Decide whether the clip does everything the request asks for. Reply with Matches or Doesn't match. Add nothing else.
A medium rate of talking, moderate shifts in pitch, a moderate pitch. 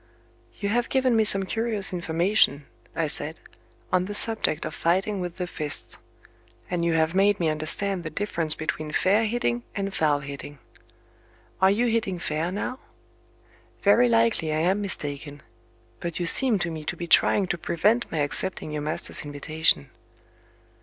Matches